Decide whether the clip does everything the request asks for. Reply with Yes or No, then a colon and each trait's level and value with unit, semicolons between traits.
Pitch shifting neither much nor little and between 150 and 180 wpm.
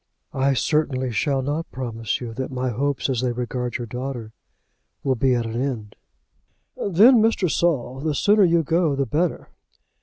Yes: average, 4.2 semitones; average, 170 wpm